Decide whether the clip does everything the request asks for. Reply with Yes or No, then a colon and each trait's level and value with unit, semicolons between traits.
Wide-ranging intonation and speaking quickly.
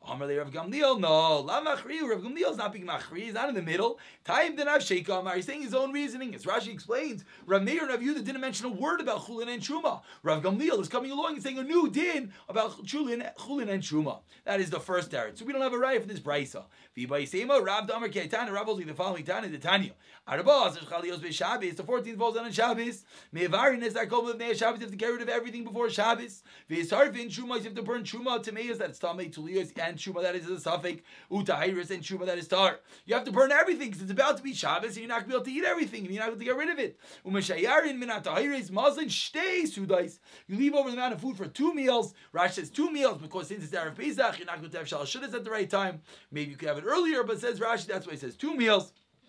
Yes: wide, 6.1 semitones; fast, 250 wpm